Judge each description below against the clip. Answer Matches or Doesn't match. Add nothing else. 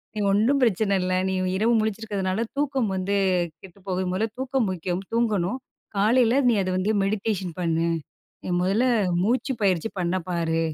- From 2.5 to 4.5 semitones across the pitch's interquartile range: Matches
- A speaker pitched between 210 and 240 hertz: Doesn't match